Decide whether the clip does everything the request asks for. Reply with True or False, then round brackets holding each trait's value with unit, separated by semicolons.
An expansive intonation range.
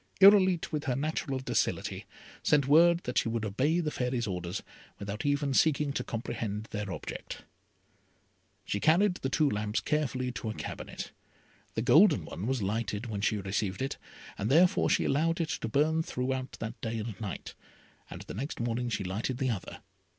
True (5.8 semitones)